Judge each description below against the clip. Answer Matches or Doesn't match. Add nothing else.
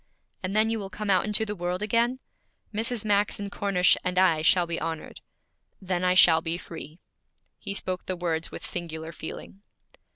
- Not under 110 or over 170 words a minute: Doesn't match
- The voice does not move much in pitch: Doesn't match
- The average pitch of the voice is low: Doesn't match